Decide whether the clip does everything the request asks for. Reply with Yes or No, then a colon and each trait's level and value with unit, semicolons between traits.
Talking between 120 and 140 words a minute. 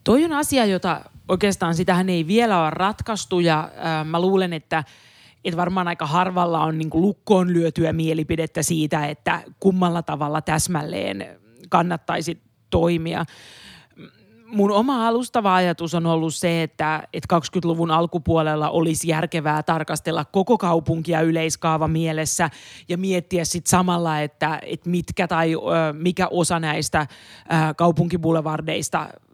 Yes: average, 130 wpm